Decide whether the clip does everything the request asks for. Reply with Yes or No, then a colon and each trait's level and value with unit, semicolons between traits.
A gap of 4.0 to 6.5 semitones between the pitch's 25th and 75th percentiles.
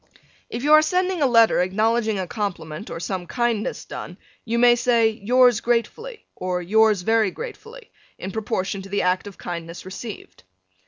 Yes: average, 4.3 semitones